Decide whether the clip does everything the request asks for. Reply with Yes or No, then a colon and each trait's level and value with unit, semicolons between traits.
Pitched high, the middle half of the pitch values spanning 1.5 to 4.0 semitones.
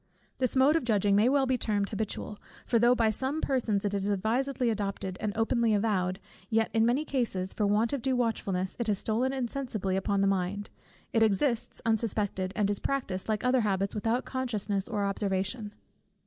Yes: high, 220 Hz; average, 3.6 semitones